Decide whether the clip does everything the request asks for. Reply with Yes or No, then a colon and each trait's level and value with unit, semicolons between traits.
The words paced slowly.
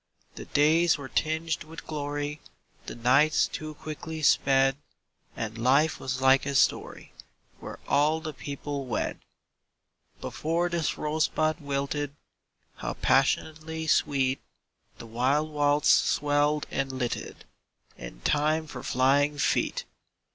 Yes: slow, 120 wpm